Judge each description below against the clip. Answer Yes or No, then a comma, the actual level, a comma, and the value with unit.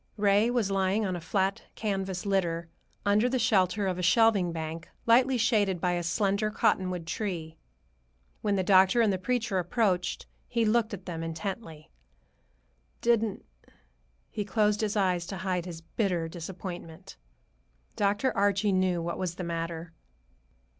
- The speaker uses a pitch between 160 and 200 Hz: Yes, high, 190 Hz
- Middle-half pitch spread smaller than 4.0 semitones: Yes, average, 3.3 semitones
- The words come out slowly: No, average, 145 wpm